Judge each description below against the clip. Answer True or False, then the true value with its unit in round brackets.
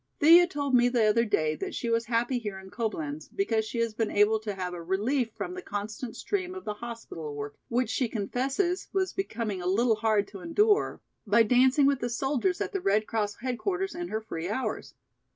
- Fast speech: True (210 wpm)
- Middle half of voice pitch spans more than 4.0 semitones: True (4.8 semitones)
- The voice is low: False (230 Hz)